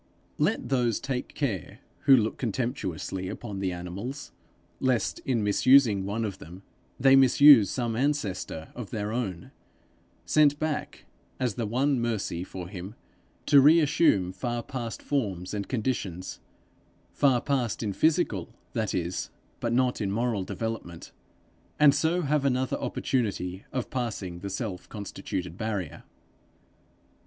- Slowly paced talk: Yes, slow, 130 wpm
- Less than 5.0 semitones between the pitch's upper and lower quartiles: No, wide, 5.4 semitones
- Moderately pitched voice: No, low, 115 Hz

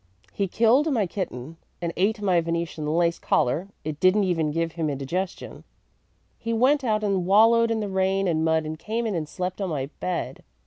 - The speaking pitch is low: No, medium, 185 Hz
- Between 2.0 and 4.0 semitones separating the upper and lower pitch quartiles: No, average, 4.6 semitones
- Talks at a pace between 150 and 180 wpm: No, average, 190 wpm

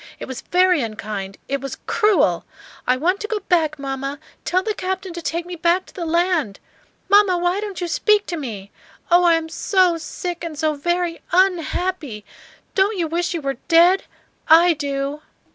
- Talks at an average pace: Yes, average, 190 wpm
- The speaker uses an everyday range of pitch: Yes, average, 4.1 semitones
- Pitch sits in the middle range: No, very high, 340 Hz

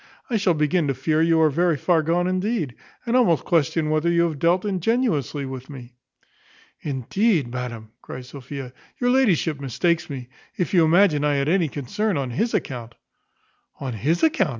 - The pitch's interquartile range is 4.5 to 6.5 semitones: Yes, average, 5.1 semitones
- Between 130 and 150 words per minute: No, average, 175 wpm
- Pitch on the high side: No, medium, 160 Hz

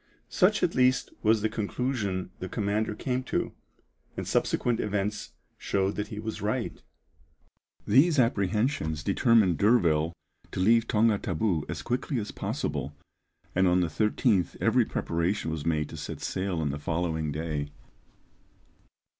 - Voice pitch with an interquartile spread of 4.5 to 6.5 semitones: Yes, average, 5.2 semitones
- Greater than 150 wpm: No, average, 140 wpm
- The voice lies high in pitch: No, low, 100 Hz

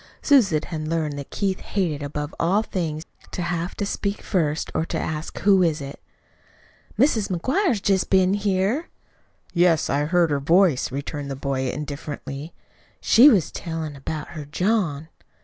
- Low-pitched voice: No, medium, 165 Hz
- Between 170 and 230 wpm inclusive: No, average, 155 wpm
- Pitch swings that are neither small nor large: Yes, average, 4.7 semitones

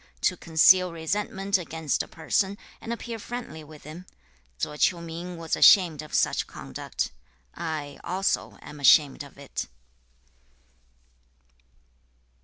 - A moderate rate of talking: No, slow, 120 wpm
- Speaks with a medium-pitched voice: Yes, medium, 165 Hz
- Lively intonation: No, average, 3.6 semitones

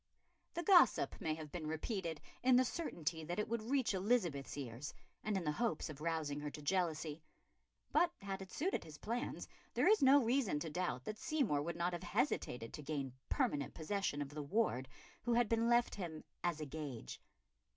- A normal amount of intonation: No, wide, 7.5 semitones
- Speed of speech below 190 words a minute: No, average, 195 wpm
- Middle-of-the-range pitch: Yes, medium, 170 Hz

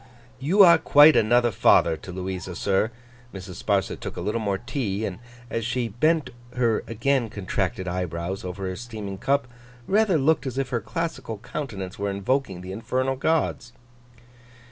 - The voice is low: Yes, low, 115 Hz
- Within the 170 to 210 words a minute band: No, average, 160 wpm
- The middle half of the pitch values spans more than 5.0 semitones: Yes, wide, 5.6 semitones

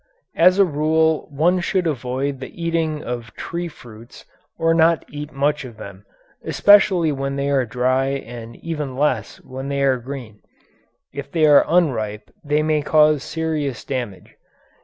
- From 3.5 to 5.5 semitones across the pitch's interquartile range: Yes, average, 3.8 semitones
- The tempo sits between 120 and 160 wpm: Yes, average, 155 wpm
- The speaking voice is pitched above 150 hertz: No, medium, 140 Hz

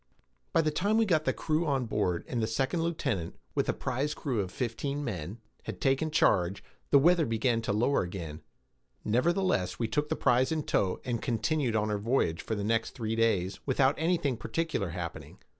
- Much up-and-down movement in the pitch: Yes, wide, 6.2 semitones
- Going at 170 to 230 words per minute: Yes, average, 190 wpm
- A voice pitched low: Yes, low, 120 Hz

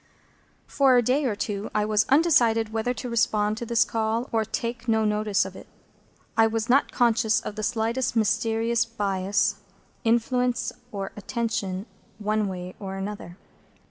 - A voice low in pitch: No, high, 225 Hz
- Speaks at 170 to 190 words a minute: No, average, 155 wpm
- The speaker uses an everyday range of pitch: No, narrow, 2.1 semitones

